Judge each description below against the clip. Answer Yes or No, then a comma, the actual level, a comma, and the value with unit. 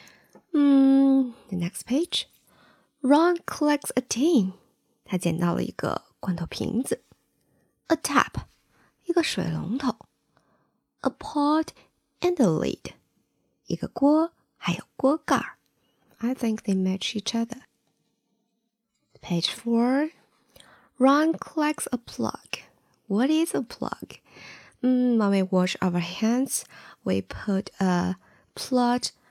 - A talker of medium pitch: No, high, 245 Hz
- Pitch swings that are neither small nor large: No, wide, 6.8 semitones